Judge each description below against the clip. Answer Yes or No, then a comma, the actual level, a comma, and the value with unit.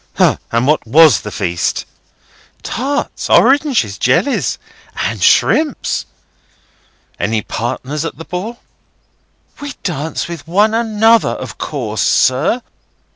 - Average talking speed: No, slow, 110 wpm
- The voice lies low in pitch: No, medium, 165 Hz